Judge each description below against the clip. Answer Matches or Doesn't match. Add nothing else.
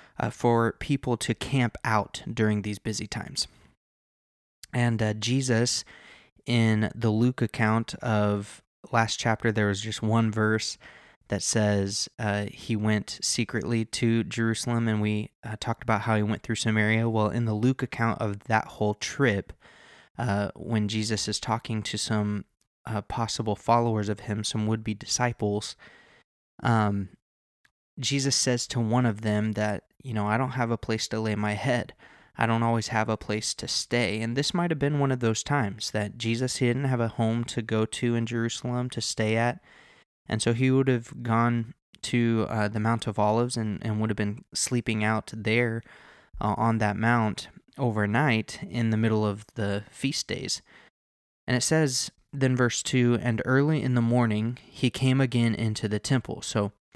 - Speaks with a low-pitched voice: Matches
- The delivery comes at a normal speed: Matches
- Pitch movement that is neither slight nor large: Doesn't match